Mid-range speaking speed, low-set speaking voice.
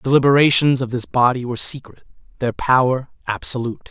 Yes: average, 155 wpm; low, 130 Hz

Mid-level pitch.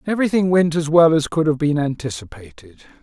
Yes: medium, 155 Hz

